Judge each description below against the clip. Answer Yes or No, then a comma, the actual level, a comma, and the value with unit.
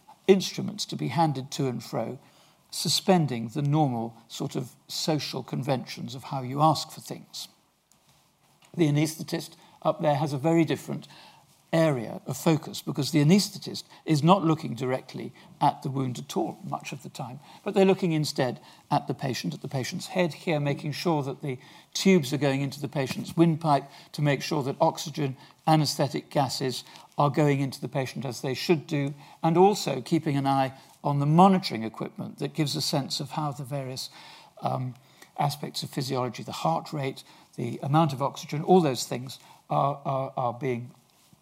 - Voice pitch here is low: No, medium, 150 Hz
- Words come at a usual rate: Yes, average, 175 wpm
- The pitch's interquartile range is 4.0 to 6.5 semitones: No, average, 3.4 semitones